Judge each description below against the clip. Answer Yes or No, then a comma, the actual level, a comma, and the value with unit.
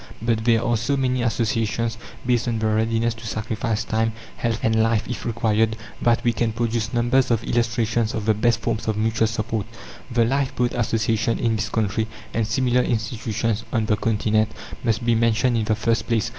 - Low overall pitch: Yes, low, 115 Hz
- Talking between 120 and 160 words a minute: No, average, 185 wpm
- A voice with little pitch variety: Yes, narrow, 1.2 semitones